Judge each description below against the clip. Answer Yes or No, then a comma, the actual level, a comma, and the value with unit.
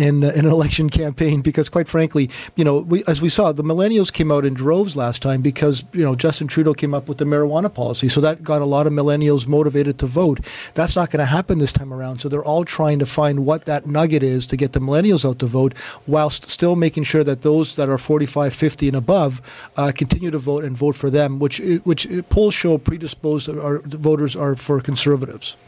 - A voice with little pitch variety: Yes, narrow, 1.9 semitones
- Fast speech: Yes, fast, 230 wpm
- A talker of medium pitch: Yes, medium, 150 Hz